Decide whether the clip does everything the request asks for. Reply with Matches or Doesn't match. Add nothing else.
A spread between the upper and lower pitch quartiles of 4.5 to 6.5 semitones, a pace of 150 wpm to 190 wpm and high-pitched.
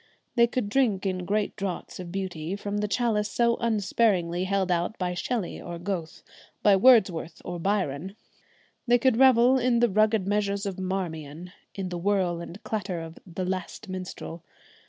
Doesn't match